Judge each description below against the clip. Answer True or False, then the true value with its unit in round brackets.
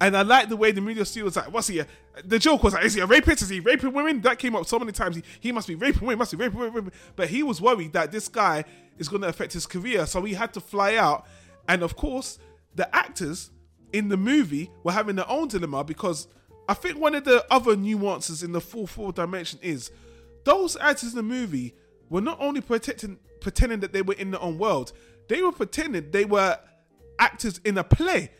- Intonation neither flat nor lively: False (5.9 semitones)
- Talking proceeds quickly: True (240 wpm)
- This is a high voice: True (200 Hz)